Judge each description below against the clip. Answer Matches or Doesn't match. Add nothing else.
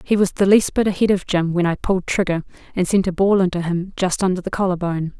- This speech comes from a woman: Matches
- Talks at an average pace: Doesn't match